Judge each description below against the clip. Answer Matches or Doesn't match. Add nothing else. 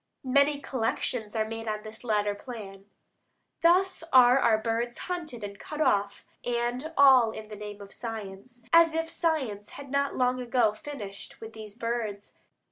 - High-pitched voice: Matches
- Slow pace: Doesn't match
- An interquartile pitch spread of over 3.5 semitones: Matches